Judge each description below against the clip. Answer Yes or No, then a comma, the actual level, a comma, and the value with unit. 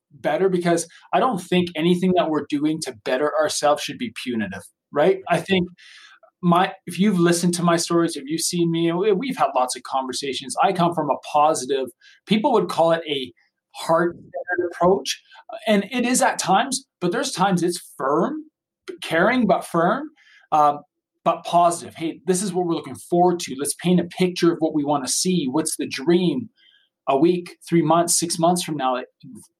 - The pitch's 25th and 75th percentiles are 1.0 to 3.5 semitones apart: Yes, average, 3.0 semitones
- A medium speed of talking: Yes, average, 190 wpm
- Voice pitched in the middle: Yes, medium, 175 Hz